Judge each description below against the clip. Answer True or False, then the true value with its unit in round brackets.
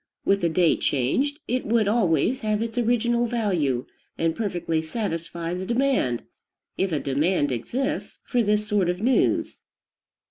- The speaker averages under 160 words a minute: True (145 wpm)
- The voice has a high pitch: True (200 Hz)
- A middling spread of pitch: False (6.3 semitones)